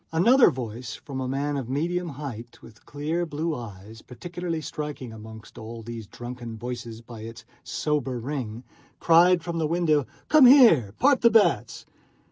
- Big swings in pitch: Yes, wide, 6.3 semitones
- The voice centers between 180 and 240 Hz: No, low, 135 Hz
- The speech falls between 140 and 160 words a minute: Yes, average, 155 wpm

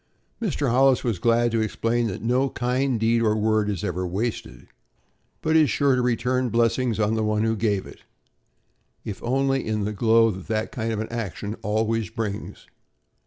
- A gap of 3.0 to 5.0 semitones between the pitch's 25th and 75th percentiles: No, narrow, 2.5 semitones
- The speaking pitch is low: Yes, low, 115 Hz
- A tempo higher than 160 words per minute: Yes, average, 170 wpm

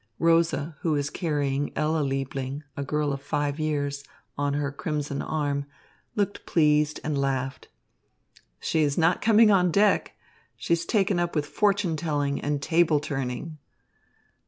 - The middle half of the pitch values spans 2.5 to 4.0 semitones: Yes, average, 2.8 semitones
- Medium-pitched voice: Yes, medium, 150 Hz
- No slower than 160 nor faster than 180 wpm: No, average, 140 wpm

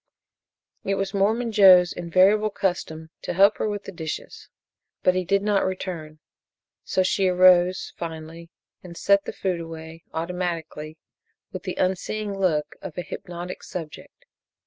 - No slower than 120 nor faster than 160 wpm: Yes, average, 145 wpm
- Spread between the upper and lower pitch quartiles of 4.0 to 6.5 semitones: No, average, 2.9 semitones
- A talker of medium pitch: Yes, medium, 180 Hz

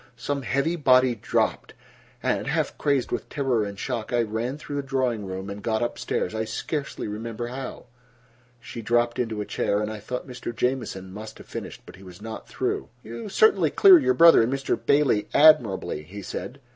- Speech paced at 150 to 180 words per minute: No, average, 190 wpm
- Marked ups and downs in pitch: No, average, 4.1 semitones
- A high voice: No, low, 120 Hz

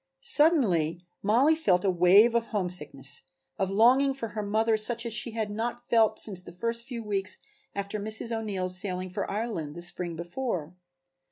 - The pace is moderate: Yes, average, 170 wpm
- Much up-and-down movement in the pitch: No, average, 4.1 semitones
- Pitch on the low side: No, high, 210 Hz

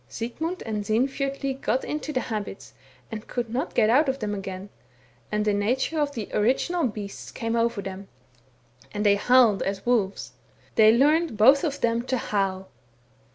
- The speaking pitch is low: No, high, 230 Hz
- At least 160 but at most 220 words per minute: Yes, average, 170 wpm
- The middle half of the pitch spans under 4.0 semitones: No, average, 4.5 semitones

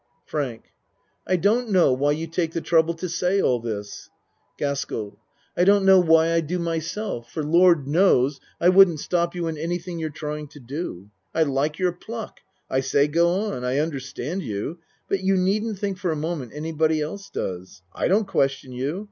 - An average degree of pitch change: Yes, average, 4.4 semitones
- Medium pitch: Yes, medium, 165 Hz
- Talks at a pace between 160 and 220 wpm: Yes, average, 190 wpm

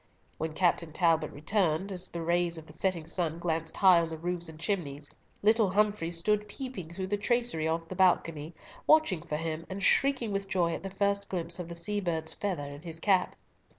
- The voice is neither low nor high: Yes, medium, 175 Hz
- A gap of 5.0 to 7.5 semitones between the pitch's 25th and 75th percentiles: No, average, 3.5 semitones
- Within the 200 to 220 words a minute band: Yes, fast, 205 wpm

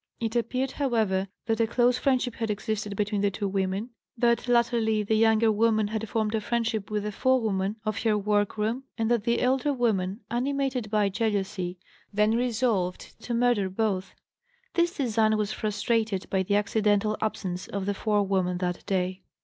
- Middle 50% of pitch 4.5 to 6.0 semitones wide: No, narrow, 2.6 semitones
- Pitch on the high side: Yes, high, 215 Hz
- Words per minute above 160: Yes, average, 170 wpm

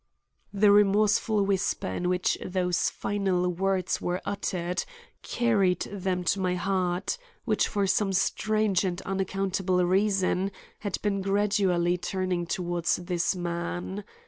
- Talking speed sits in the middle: No, slow, 120 wpm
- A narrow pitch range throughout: Yes, narrow, 1.9 semitones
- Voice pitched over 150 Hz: Yes, high, 190 Hz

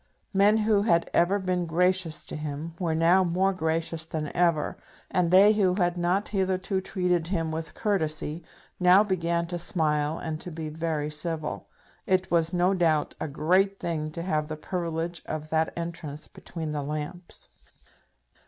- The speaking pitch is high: No, medium, 170 Hz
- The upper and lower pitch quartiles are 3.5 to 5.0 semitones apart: No, average, 2.7 semitones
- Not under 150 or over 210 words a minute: Yes, average, 160 wpm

